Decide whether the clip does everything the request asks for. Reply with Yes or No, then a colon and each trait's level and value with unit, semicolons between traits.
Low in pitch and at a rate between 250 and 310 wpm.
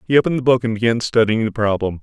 Yes: low, 115 Hz; fast, 265 wpm